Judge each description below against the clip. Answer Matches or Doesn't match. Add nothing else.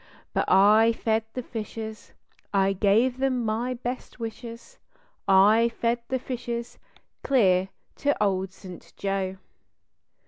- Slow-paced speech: Matches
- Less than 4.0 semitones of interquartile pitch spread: Matches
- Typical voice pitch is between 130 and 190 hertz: Doesn't match